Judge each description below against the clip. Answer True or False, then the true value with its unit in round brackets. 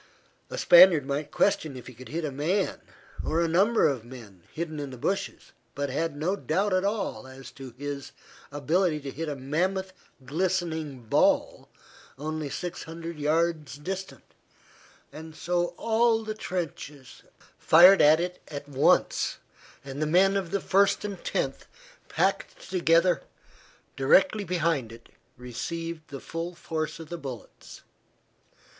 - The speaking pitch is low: False (160 Hz)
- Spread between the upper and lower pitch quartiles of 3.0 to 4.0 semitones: False (4.5 semitones)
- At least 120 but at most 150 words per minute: True (145 wpm)